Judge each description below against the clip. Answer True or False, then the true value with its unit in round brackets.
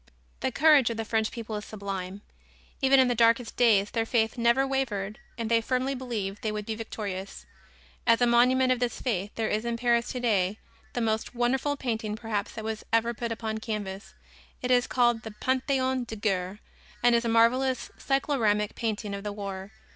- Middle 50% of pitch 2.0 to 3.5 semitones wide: True (2.7 semitones)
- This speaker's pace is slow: False (190 wpm)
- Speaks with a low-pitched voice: False (230 Hz)